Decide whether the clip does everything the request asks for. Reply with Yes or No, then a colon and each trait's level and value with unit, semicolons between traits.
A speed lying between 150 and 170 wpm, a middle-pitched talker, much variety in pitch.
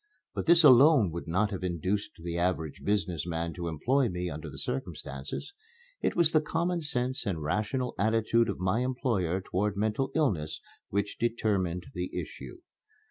No: average, 160 wpm; low, 100 Hz; wide, 6.3 semitones